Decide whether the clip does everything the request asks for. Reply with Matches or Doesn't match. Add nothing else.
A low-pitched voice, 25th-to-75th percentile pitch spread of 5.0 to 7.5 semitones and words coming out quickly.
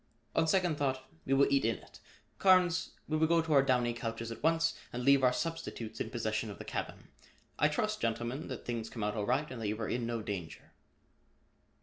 Matches